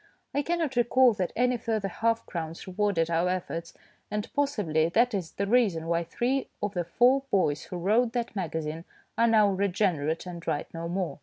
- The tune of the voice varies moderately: No, wide, 5.7 semitones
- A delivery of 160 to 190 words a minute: Yes, average, 180 wpm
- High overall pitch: Yes, high, 195 Hz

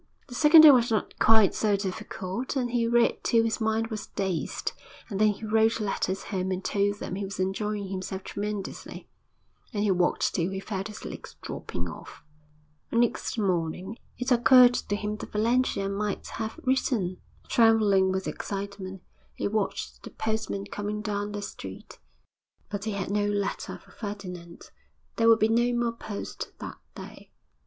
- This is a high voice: Yes, high, 210 Hz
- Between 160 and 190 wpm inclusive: Yes, average, 165 wpm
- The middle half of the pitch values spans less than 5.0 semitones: Yes, narrow, 2.6 semitones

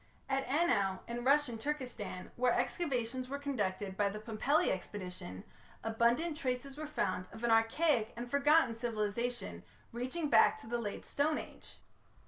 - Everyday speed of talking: Yes, average, 145 wpm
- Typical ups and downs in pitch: Yes, average, 4.9 semitones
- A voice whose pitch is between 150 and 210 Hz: No, high, 240 Hz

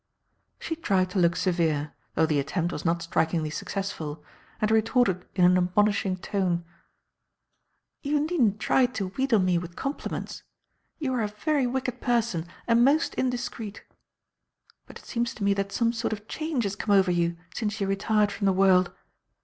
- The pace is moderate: Yes, average, 170 wpm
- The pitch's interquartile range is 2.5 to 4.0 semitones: No, average, 4.9 semitones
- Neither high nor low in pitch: No, high, 200 Hz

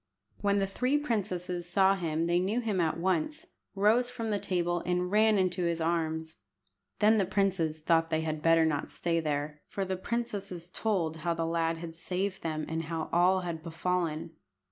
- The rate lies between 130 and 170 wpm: No, average, 185 wpm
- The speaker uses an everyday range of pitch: Yes, average, 3.2 semitones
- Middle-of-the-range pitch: Yes, medium, 175 Hz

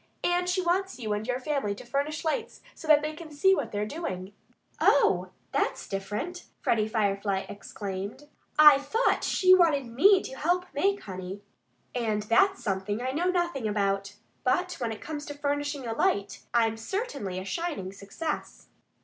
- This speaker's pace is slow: No, average, 165 wpm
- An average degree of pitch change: No, wide, 8.2 semitones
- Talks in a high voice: Yes, very high, 265 Hz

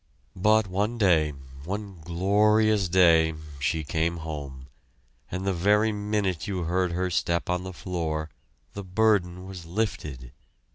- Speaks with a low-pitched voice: Yes, very low, 90 Hz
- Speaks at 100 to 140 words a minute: Yes, slow, 135 wpm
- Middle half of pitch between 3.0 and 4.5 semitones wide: Yes, average, 3.7 semitones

